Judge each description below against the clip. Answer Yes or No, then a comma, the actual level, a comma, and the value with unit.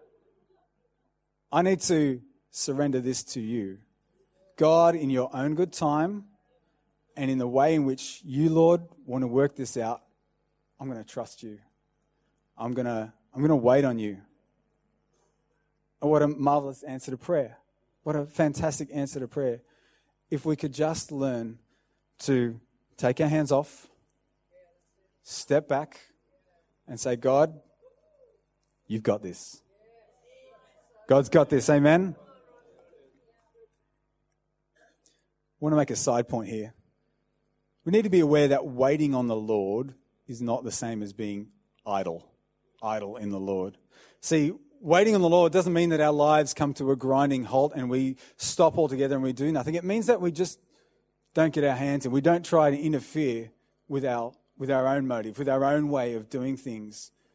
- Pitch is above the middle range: No, medium, 140 Hz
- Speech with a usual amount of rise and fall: Yes, average, 4.1 semitones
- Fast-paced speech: No, average, 160 wpm